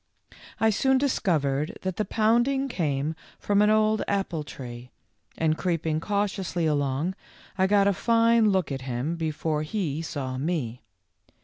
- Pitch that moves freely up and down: Yes, wide, 6.0 semitones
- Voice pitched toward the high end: No, medium, 170 Hz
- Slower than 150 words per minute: Yes, average, 140 wpm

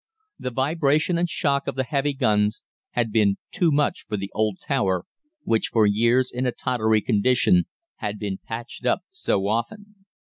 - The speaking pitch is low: Yes, low, 120 Hz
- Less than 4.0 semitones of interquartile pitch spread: No, average, 5.0 semitones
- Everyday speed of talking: Yes, average, 170 wpm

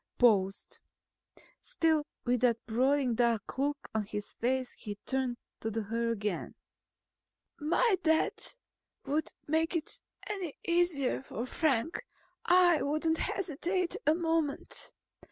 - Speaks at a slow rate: Yes, slow, 120 wpm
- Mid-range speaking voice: No, very high, 280 Hz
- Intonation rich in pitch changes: Yes, wide, 5.7 semitones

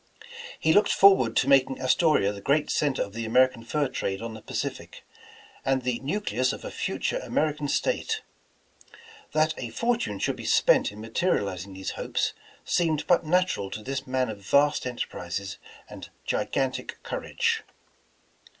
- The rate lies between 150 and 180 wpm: Yes, average, 160 wpm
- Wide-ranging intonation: Yes, wide, 5.8 semitones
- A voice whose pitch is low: Yes, low, 130 Hz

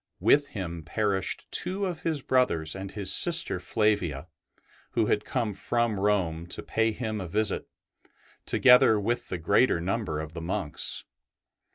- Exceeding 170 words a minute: No, average, 150 wpm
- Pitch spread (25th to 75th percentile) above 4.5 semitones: Yes, average, 5.2 semitones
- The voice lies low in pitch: Yes, low, 105 Hz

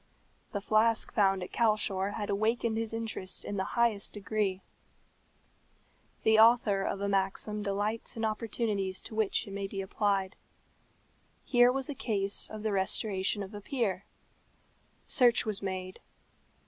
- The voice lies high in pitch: Yes, high, 205 Hz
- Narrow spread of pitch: Yes, narrow, 2.3 semitones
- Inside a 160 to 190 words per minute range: No, average, 145 wpm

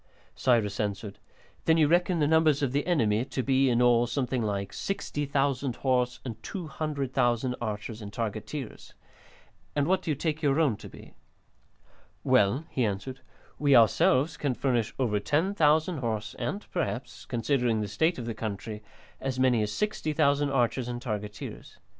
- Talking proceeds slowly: No, average, 155 wpm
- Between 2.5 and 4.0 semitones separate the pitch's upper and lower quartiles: No, average, 4.7 semitones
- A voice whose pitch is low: Yes, low, 130 Hz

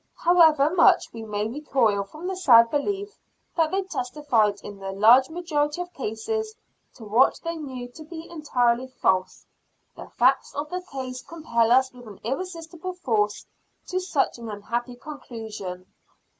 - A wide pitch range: Yes, wide, 6.5 semitones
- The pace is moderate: Yes, average, 155 wpm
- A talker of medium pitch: No, very high, 265 Hz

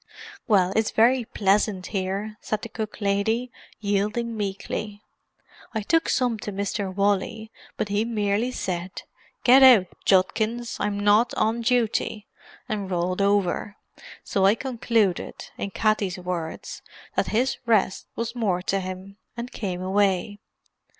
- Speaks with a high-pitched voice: Yes, high, 205 Hz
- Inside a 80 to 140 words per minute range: Yes, slow, 135 wpm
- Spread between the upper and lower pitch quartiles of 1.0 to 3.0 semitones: Yes, average, 2.7 semitones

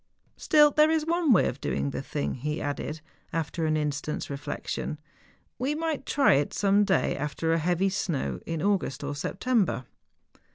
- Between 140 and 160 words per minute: No, average, 170 wpm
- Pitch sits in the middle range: Yes, medium, 165 Hz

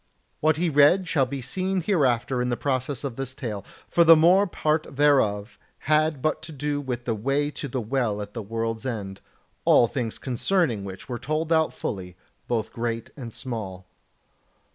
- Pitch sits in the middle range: No, low, 130 Hz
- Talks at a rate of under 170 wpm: No, average, 180 wpm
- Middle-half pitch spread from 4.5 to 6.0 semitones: Yes, average, 5.1 semitones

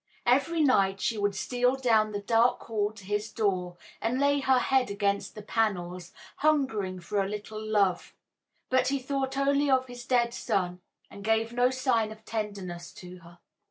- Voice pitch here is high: Yes, high, 220 Hz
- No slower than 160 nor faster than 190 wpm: Yes, average, 175 wpm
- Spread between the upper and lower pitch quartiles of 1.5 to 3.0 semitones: No, average, 4.3 semitones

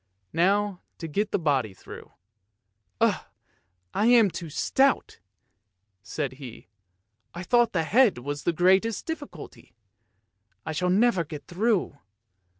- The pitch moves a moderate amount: No, wide, 6.7 semitones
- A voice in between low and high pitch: Yes, medium, 175 Hz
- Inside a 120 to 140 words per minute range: Yes, slow, 135 wpm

